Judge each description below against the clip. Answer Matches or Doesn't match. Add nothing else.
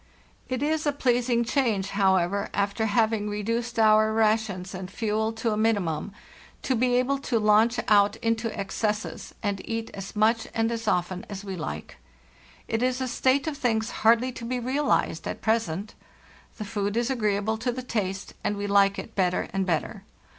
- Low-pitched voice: Doesn't match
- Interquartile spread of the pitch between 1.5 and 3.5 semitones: Matches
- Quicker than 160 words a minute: Matches